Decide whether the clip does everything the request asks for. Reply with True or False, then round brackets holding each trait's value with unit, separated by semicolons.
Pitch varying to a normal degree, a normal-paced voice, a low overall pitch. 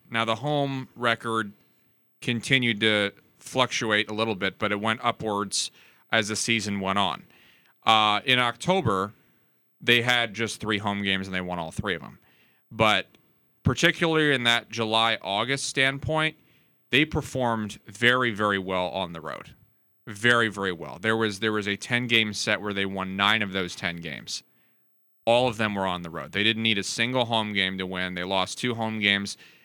True (3.2 semitones; 180 wpm; 110 Hz)